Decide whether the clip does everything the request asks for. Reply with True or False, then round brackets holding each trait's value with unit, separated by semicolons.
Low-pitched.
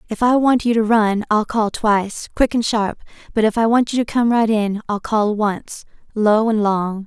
False (220 Hz)